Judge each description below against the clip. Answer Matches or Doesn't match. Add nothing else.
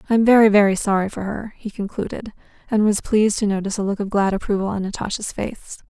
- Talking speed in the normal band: Doesn't match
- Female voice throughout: Matches